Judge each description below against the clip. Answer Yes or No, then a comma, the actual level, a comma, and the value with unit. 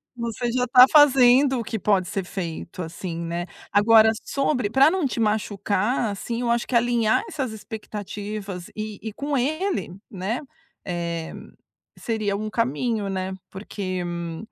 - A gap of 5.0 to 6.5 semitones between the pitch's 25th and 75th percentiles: No, average, 4.3 semitones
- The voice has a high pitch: Yes, high, 215 Hz